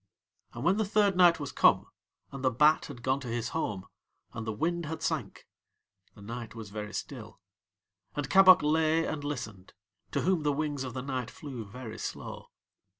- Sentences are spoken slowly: No, average, 185 wpm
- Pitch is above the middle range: No, medium, 140 Hz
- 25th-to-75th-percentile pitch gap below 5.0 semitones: No, wide, 5.5 semitones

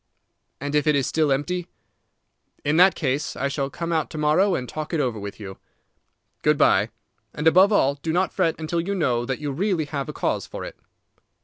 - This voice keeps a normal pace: No, fast, 210 wpm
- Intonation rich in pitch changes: No, average, 3.6 semitones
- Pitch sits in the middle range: Yes, medium, 150 Hz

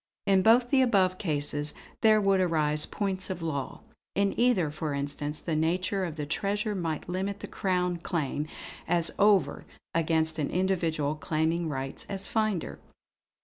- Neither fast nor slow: Yes, average, 150 wpm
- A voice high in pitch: No, medium, 175 Hz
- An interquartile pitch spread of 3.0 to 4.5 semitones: Yes, average, 4.2 semitones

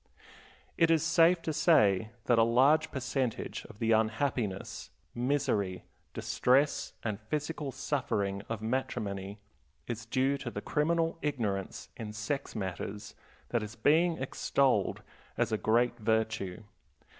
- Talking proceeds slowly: Yes, slow, 125 wpm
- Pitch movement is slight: No, average, 5.3 semitones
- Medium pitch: No, low, 120 Hz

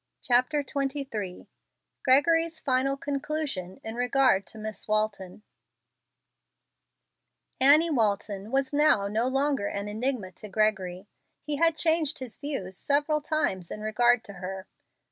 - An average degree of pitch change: No, wide, 5.9 semitones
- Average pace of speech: No, slow, 125 wpm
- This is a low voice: No, very high, 250 Hz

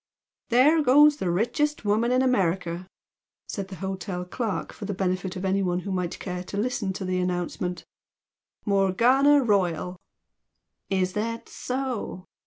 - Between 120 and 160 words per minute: Yes, average, 140 wpm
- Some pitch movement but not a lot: Yes, average, 4.9 semitones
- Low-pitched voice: No, high, 195 Hz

